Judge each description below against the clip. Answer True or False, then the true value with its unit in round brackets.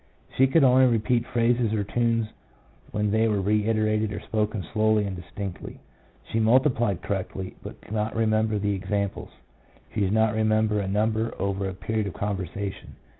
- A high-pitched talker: False (110 Hz)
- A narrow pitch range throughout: True (1.9 semitones)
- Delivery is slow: False (160 wpm)